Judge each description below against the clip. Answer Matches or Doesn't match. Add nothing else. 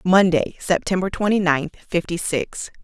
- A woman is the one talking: Matches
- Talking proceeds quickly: Doesn't match